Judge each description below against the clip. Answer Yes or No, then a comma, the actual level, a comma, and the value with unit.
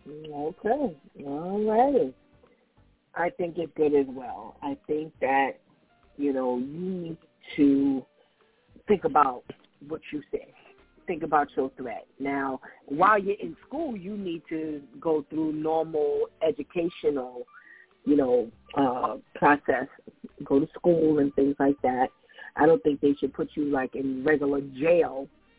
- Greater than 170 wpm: No, average, 140 wpm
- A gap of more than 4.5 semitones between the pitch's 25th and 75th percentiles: No, average, 4.1 semitones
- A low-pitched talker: No, medium, 155 Hz